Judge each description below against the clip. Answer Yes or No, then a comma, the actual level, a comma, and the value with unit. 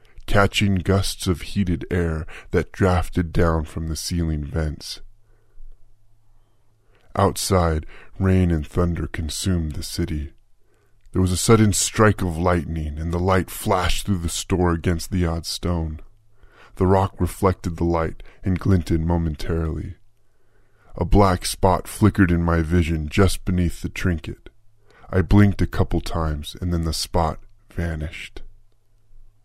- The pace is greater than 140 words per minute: No, slow, 135 wpm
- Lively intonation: No, average, 3.9 semitones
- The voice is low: Yes, very low, 90 Hz